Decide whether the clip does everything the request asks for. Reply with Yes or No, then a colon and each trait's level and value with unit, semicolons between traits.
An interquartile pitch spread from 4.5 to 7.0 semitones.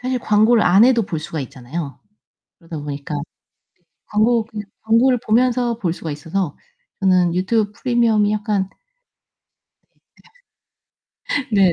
Yes: wide, 5.4 semitones